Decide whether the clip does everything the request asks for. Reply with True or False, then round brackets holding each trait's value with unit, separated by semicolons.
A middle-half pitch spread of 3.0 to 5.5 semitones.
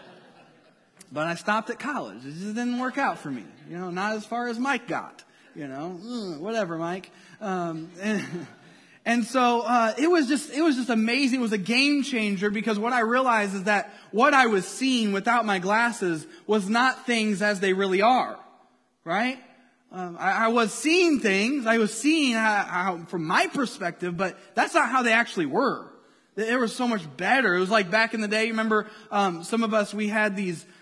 True (3.9 semitones)